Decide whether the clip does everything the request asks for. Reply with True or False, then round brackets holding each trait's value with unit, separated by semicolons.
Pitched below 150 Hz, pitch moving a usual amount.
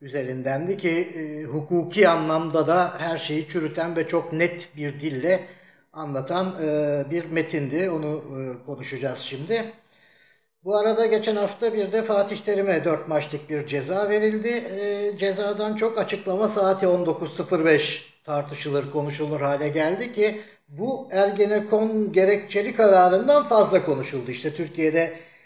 False (170 Hz; 5.0 semitones)